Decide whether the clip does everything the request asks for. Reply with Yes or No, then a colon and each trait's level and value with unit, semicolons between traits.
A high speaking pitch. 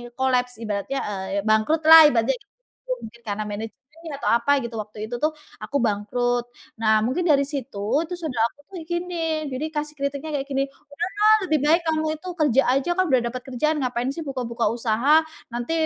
Yes: very high, 260 Hz